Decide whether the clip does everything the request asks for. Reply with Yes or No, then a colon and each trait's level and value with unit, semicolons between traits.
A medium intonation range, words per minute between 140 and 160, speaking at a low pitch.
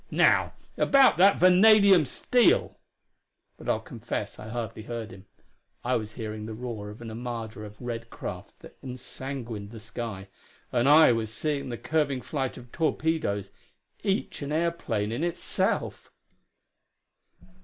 No: wide, 5.9 semitones; average, 145 wpm; low, 120 Hz